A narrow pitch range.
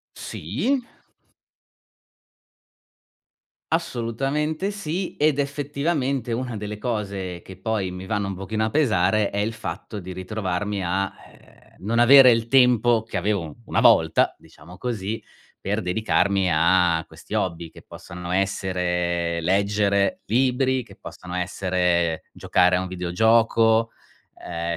No: average, 4.9 semitones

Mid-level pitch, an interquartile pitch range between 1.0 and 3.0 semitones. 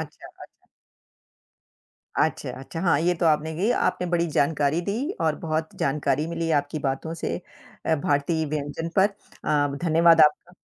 Yes: medium, 160 Hz; narrow, 2.5 semitones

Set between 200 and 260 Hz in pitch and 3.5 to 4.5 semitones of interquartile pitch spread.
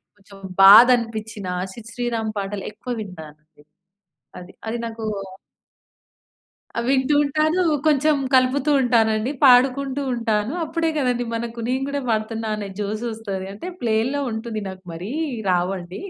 Yes: high, 225 Hz; average, 3.9 semitones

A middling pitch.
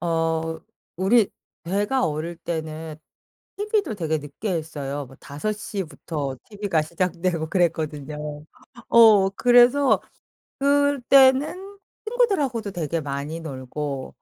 Yes: medium, 170 Hz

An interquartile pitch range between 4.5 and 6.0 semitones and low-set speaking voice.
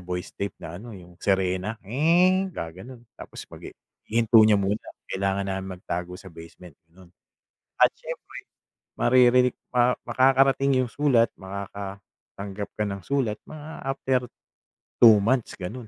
Yes: average, 5.1 semitones; low, 105 Hz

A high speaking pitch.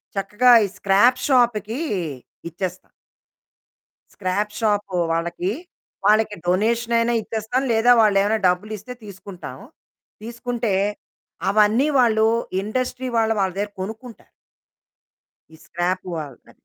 Yes: high, 215 Hz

